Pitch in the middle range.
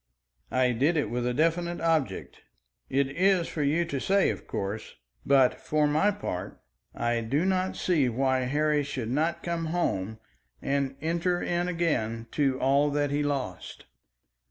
Yes: medium, 145 Hz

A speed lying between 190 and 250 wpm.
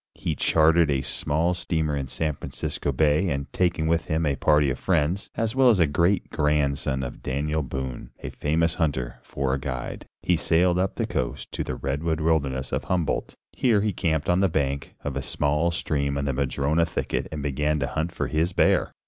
Yes: average, 200 wpm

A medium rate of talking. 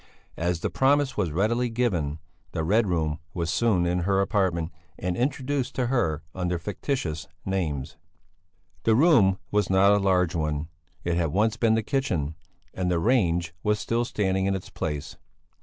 Yes: average, 165 wpm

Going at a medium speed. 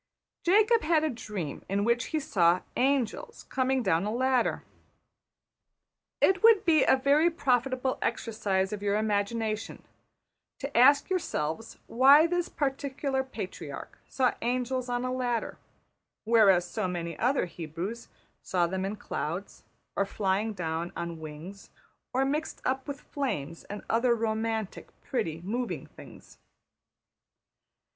No: slow, 130 wpm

